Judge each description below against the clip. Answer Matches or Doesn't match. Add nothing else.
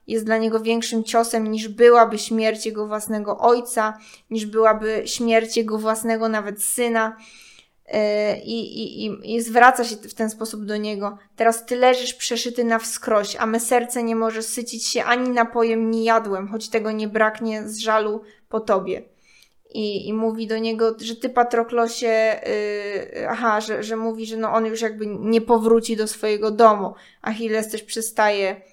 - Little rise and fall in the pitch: Matches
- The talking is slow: Doesn't match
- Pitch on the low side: Doesn't match